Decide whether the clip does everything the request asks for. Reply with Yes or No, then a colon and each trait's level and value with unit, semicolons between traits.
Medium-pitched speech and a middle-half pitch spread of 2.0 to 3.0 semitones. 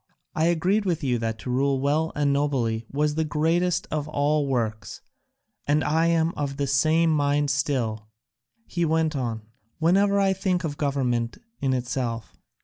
No: medium, 145 Hz; average, 3.8 semitones